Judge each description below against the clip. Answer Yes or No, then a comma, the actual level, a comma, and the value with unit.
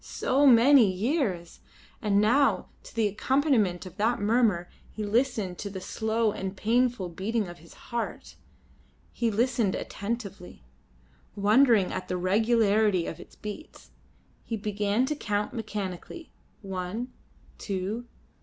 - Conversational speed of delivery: No, slow, 125 wpm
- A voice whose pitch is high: Yes, high, 210 Hz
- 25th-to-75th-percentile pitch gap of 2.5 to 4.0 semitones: Yes, average, 3.7 semitones